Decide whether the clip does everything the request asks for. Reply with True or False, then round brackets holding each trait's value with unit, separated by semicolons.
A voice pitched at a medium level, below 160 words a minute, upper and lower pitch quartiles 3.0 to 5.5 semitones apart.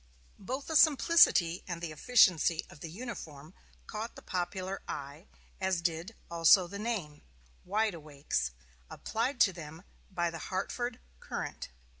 True (180 Hz; 135 wpm; 5.1 semitones)